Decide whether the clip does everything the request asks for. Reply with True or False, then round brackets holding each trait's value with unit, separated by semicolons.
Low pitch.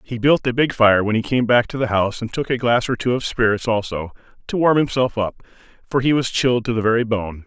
True (115 Hz)